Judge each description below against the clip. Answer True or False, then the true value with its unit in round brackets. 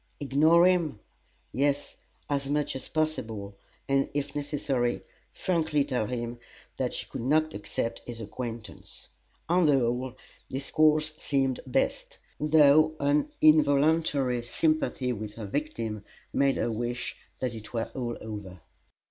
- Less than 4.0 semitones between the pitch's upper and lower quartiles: False (4.4 semitones)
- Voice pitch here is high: False (135 Hz)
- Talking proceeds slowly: True (130 wpm)